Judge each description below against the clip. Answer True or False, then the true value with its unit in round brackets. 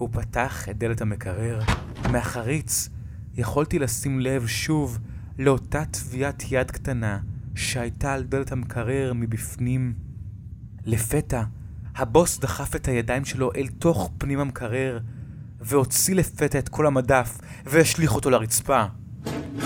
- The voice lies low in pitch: True (125 Hz)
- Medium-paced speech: True (115 wpm)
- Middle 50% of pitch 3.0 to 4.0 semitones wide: True (3.3 semitones)